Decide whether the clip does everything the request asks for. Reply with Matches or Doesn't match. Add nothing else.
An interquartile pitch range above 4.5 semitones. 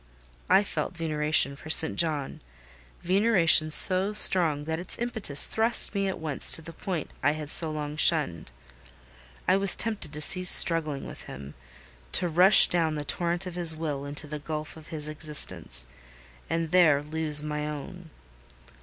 Doesn't match